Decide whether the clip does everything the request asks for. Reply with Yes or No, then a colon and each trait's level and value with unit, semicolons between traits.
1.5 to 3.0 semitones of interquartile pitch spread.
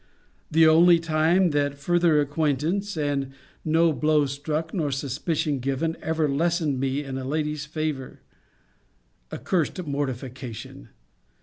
Yes: average, 2.7 semitones